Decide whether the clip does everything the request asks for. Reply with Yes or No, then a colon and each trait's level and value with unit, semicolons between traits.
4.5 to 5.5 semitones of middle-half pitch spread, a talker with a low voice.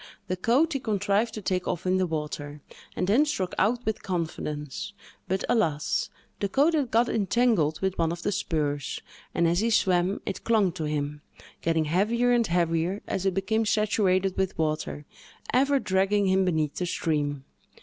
No: average, 5.1 semitones; medium, 185 Hz